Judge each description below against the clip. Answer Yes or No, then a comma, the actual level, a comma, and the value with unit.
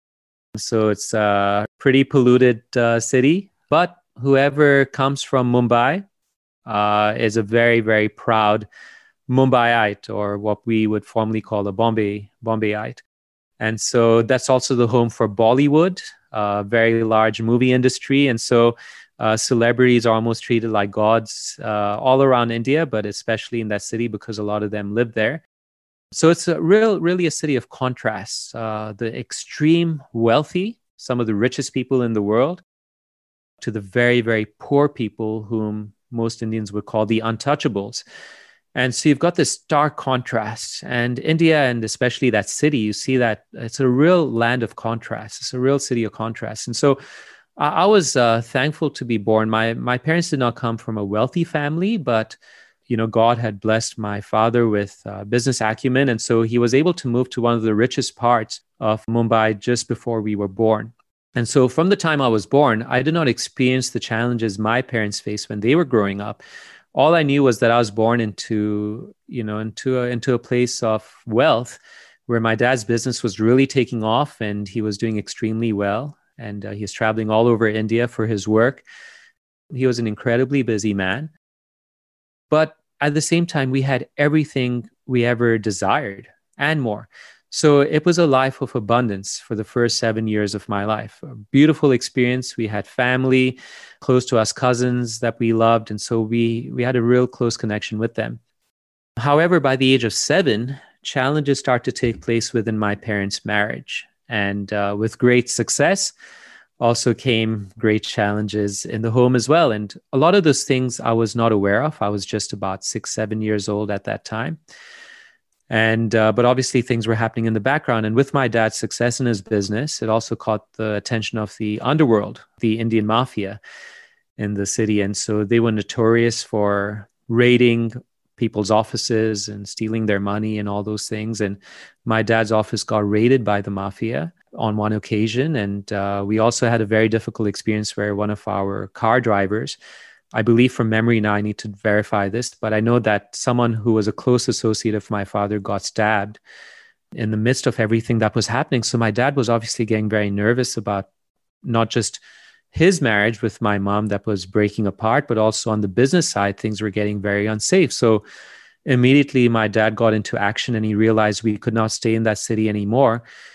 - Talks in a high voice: No, low, 115 Hz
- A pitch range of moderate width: Yes, average, 3.0 semitones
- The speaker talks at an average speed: Yes, average, 190 wpm